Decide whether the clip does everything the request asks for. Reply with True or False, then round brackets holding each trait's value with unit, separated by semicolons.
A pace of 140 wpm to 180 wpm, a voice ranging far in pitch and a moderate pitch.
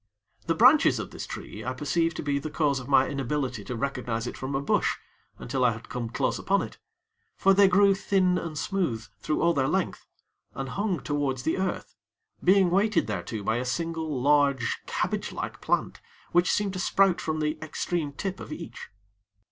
False (190 wpm; 5.8 semitones; 145 Hz)